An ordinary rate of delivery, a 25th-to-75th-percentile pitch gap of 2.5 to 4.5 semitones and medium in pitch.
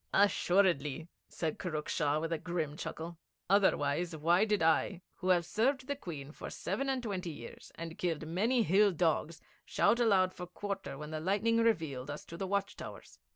Yes: average, 180 wpm; average, 4.1 semitones; medium, 175 Hz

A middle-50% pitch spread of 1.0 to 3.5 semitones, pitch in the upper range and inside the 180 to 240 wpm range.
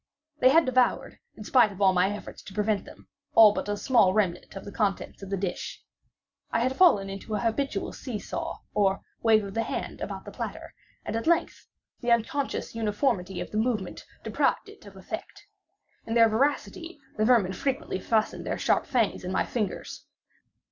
No: average, 4.1 semitones; high, 215 Hz; average, 190 wpm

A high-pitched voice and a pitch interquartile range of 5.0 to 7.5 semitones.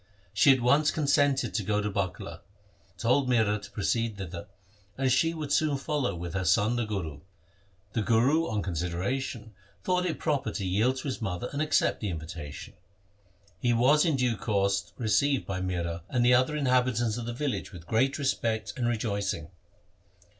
No: low, 115 Hz; average, 5.3 semitones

